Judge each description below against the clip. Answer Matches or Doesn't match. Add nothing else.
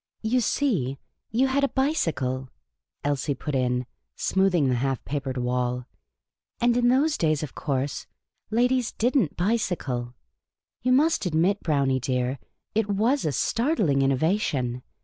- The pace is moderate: Matches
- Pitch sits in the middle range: Matches